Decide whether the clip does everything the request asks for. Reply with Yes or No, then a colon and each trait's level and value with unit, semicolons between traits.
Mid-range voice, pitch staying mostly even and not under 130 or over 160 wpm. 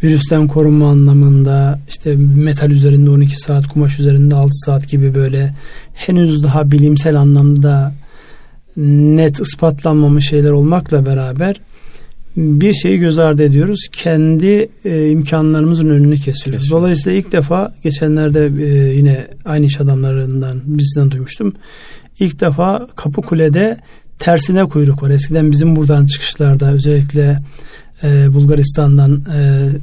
No: medium, 145 Hz; narrow, 2.1 semitones; average, 115 wpm